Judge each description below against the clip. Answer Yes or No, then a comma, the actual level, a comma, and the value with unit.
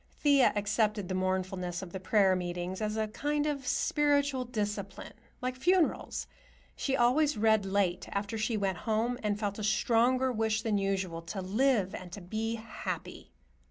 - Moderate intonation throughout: Yes, average, 4.4 semitones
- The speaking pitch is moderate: No, high, 215 Hz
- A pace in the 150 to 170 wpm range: Yes, average, 160 wpm